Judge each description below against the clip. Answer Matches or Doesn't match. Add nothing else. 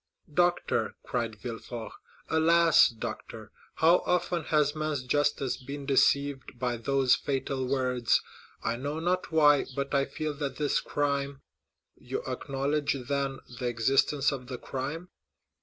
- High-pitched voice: Doesn't match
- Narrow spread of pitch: Matches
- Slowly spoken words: Matches